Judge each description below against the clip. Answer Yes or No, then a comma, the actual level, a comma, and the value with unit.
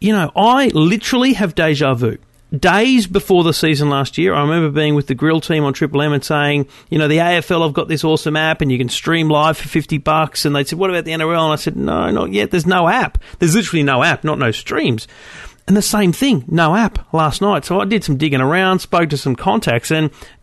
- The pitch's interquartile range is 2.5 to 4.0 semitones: Yes, average, 3.7 semitones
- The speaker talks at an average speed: No, fast, 245 wpm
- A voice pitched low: No, medium, 160 Hz